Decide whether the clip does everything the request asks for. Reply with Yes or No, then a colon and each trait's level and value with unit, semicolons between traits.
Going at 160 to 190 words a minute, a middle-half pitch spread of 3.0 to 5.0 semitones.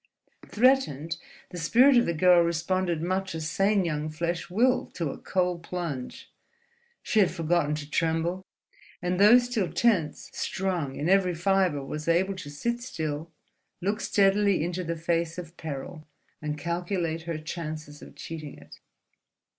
No: average, 150 wpm; average, 3.3 semitones